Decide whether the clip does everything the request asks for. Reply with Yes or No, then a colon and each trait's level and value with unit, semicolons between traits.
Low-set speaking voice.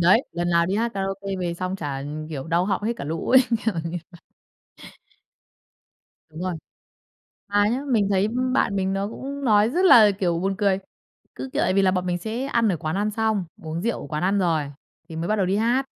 No: high, 195 Hz